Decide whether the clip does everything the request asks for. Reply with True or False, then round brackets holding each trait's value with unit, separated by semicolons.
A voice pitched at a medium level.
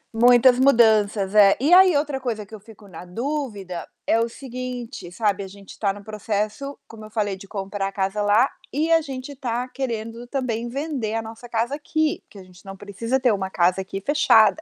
False (225 Hz)